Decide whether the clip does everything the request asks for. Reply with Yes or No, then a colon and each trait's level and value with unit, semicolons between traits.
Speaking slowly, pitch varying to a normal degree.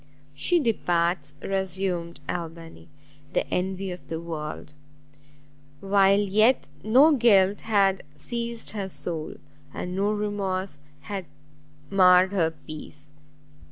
Yes: slow, 105 wpm; average, 3.4 semitones